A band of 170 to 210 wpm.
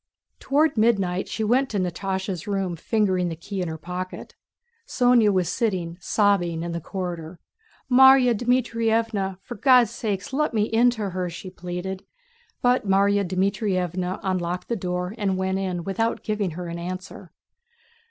No: average, 150 wpm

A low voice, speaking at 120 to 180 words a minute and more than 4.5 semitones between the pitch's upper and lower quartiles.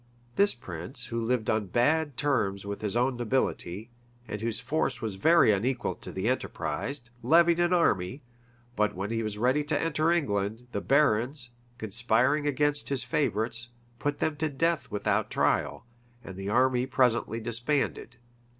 Yes: low, 120 Hz; average, 155 wpm; average, 5.1 semitones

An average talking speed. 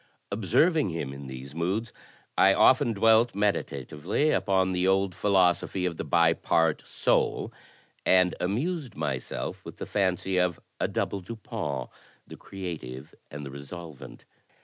Yes: average, 145 wpm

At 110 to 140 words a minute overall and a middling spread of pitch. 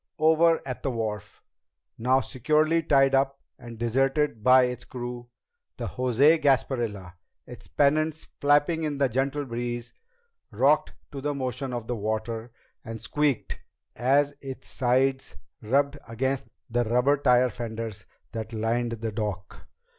Yes: slow, 135 wpm; average, 3.4 semitones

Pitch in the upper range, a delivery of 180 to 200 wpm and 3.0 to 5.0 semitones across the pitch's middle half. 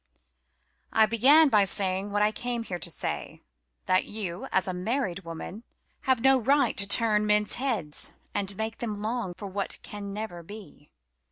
No: high, 210 Hz; average, 170 wpm; average, 3.4 semitones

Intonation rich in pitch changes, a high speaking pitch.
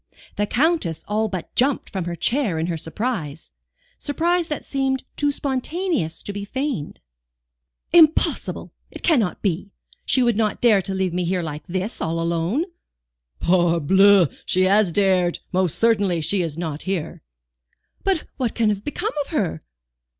Yes: wide, 7.1 semitones; high, 200 Hz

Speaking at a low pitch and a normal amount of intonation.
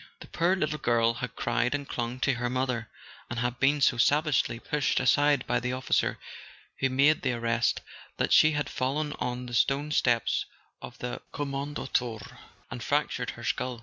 Yes: low, 125 Hz; average, 3.1 semitones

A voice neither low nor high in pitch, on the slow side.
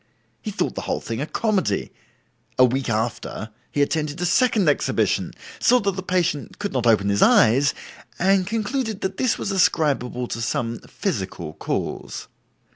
No: medium, 150 Hz; average, 160 wpm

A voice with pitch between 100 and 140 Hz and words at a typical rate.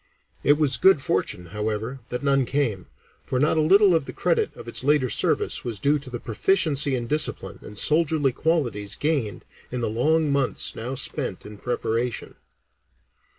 Yes: low, 135 Hz; average, 170 wpm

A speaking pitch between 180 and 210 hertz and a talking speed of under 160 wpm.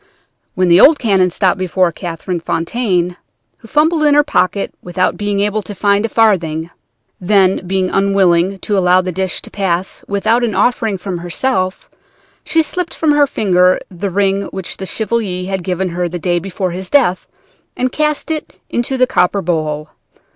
No: high, 190 Hz; average, 175 wpm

